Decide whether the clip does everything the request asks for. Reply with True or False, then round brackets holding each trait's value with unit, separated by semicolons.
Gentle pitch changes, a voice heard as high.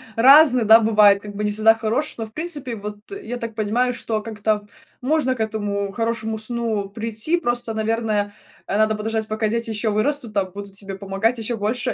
True (2.1 semitones; 220 Hz)